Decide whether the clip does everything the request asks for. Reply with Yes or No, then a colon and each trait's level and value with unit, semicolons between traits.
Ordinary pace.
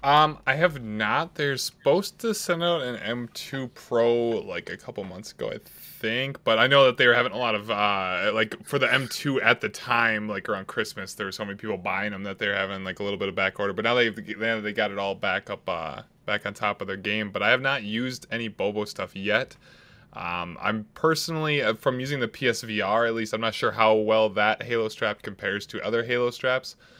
No: fast, 235 wpm